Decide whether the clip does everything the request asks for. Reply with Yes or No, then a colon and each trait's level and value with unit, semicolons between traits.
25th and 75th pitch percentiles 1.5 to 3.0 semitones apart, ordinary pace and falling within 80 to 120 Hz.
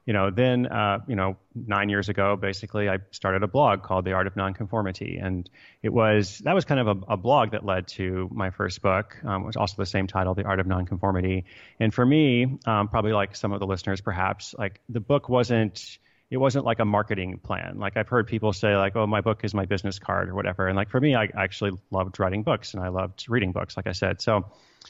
No: narrow, 2.6 semitones; fast, 240 wpm; low, 100 Hz